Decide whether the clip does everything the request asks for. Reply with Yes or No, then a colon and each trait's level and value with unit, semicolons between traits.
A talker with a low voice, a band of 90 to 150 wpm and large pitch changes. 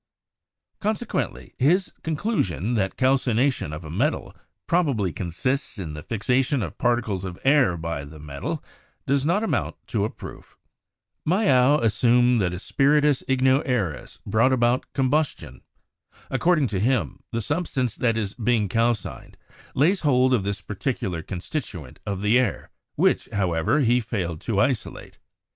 Yes: low, 120 Hz; average, 140 wpm; wide, 6.1 semitones